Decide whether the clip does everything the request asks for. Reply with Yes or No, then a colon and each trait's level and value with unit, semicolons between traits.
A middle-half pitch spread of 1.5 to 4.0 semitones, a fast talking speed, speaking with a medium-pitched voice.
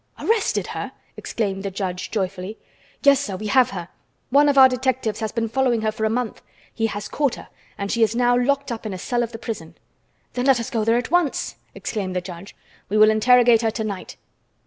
No: average, 3.4 semitones; fast, 220 wpm; high, 225 Hz